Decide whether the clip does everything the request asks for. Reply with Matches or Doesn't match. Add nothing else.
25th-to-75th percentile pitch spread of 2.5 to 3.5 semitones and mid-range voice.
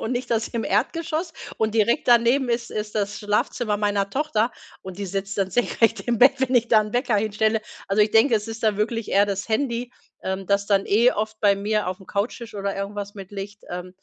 Doesn't match